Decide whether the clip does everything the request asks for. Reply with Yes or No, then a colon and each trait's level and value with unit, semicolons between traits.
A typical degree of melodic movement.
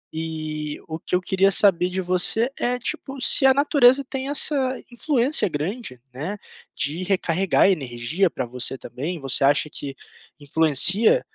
No: wide, 8.3 semitones